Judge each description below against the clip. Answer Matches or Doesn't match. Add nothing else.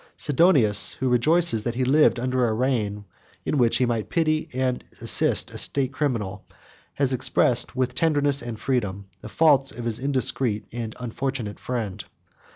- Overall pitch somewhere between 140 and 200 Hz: Doesn't match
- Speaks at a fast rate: Doesn't match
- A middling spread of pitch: Matches